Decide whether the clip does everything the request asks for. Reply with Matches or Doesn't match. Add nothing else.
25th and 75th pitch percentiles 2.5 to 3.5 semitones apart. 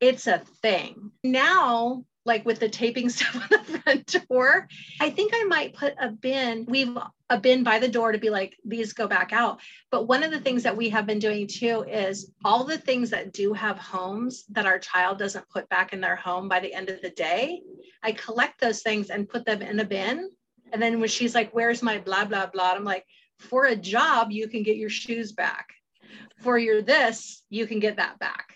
Matches